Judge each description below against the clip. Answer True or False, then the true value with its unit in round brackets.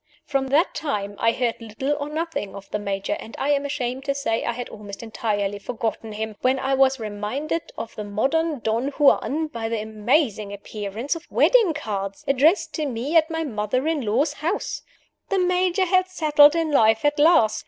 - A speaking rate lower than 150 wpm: False (190 wpm)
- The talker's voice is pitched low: False (265 Hz)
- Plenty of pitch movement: True (5.9 semitones)